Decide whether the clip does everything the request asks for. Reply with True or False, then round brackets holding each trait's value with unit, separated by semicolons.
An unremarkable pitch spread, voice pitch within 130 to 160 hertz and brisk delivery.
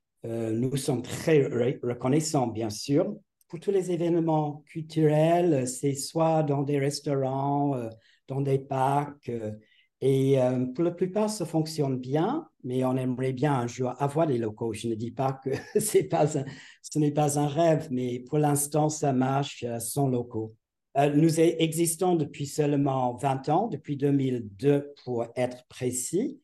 False (3.4 semitones; 140 Hz; 150 wpm)